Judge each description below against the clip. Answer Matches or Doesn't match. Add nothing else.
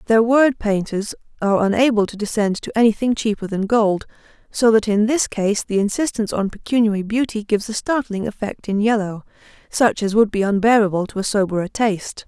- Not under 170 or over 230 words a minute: Matches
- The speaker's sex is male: Doesn't match